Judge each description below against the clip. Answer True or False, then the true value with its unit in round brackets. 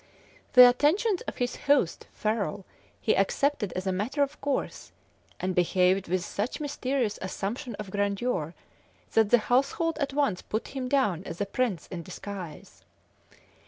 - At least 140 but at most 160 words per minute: True (150 wpm)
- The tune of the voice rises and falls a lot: True (6.5 semitones)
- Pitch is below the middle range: False (215 Hz)